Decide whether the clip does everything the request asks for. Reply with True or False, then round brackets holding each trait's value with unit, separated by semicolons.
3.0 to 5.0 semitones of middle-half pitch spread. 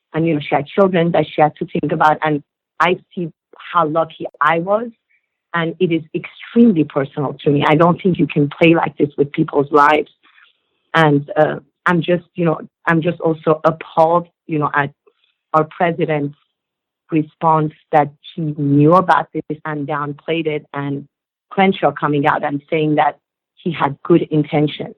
False (2.4 semitones)